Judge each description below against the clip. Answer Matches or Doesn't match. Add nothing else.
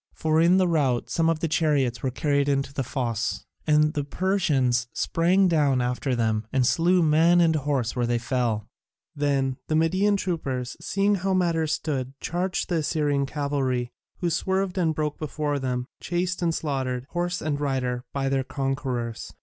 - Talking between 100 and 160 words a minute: Doesn't match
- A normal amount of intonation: Matches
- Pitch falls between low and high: Matches